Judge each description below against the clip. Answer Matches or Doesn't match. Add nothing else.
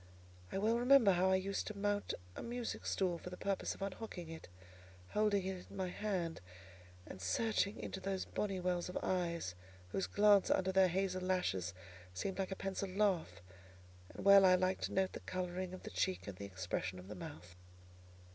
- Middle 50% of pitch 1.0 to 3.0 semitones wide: Matches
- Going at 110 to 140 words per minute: Doesn't match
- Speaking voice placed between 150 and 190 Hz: Matches